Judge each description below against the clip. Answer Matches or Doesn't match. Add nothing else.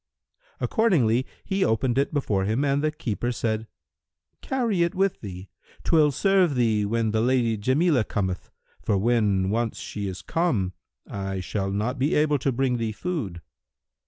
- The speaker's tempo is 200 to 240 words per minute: Doesn't match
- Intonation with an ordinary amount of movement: Doesn't match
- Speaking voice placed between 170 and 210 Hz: Doesn't match